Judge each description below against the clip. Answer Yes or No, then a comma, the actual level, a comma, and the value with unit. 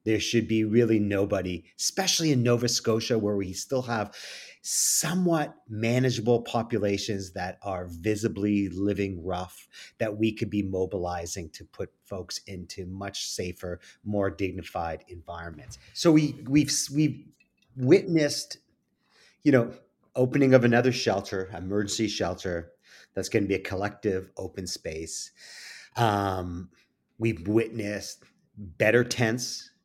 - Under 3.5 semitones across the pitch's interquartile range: No, average, 4.0 semitones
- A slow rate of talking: Yes, slow, 125 wpm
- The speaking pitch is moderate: No, low, 105 Hz